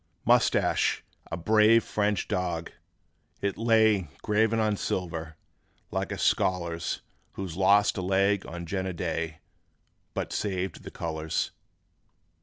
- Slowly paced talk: Yes, slow, 115 wpm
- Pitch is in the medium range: No, very low, 95 Hz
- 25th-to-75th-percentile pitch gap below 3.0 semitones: No, average, 3.7 semitones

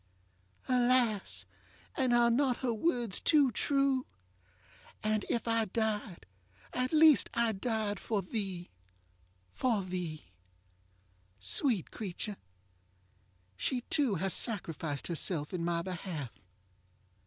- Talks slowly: Yes, slow, 105 wpm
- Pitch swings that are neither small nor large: No, wide, 6.0 semitones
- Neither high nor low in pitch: No, high, 210 Hz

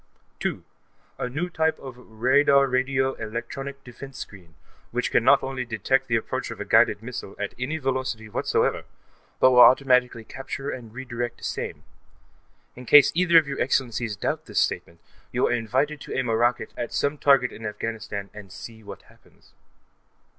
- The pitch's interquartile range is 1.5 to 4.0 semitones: Yes, average, 3.1 semitones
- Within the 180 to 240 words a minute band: No, average, 170 wpm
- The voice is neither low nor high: No, low, 125 Hz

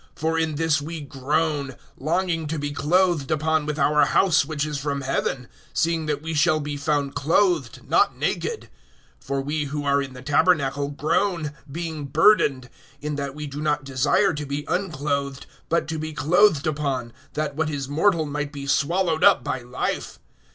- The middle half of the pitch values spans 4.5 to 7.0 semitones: No, narrow, 2.4 semitones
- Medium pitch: Yes, medium, 150 Hz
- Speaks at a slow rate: No, average, 175 wpm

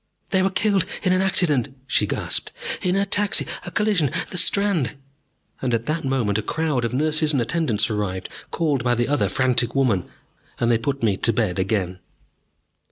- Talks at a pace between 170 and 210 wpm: Yes, average, 185 wpm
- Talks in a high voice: No, low, 135 Hz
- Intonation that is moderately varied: No, wide, 6.5 semitones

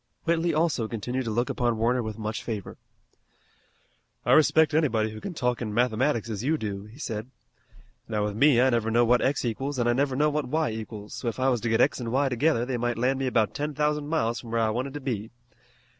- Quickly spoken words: Yes, fast, 235 wpm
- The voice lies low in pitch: Yes, low, 120 Hz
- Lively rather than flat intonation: No, average, 4.1 semitones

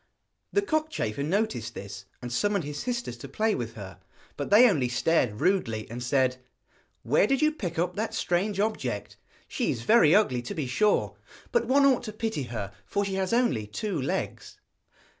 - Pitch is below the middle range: No, medium, 170 Hz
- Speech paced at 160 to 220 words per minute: Yes, average, 180 wpm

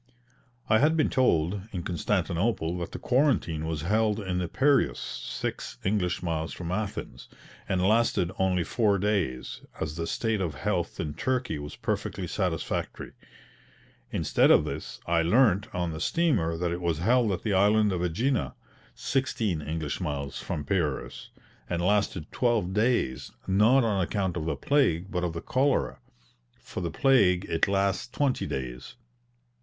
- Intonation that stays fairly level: No, average, 5.0 semitones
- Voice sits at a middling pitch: No, very low, 95 Hz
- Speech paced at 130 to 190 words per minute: Yes, average, 155 wpm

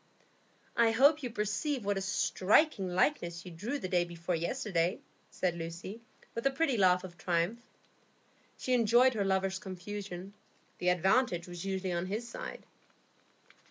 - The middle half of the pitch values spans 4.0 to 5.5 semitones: Yes, average, 4.7 semitones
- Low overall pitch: No, high, 195 Hz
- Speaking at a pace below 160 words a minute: Yes, average, 150 wpm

